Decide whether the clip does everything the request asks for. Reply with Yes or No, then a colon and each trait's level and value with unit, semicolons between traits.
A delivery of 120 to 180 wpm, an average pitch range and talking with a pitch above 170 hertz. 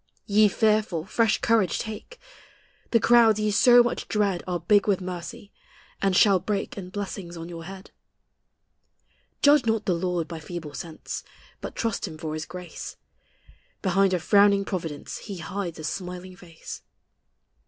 Yes: average, 155 wpm; average, 3.5 semitones; high, 190 Hz